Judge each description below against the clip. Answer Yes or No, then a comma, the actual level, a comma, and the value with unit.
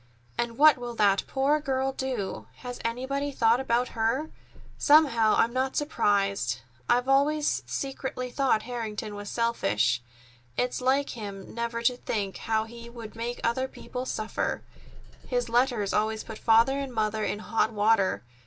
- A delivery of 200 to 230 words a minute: No, average, 150 wpm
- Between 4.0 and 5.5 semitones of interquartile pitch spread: No, average, 3.3 semitones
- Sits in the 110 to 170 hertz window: No, high, 235 Hz